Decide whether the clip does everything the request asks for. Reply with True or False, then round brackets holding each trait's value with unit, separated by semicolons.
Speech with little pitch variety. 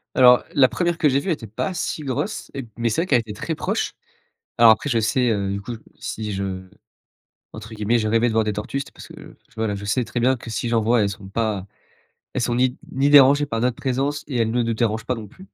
False (3.5 semitones)